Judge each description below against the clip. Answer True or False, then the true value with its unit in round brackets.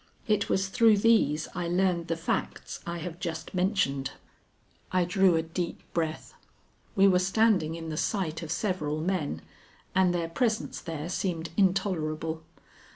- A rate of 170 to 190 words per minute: False (150 wpm)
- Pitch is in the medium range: True (175 Hz)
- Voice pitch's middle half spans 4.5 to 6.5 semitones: False (3.0 semitones)